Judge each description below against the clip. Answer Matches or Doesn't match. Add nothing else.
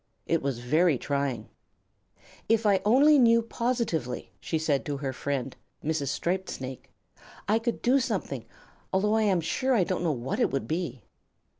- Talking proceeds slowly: Doesn't match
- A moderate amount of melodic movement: Doesn't match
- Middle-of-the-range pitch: Matches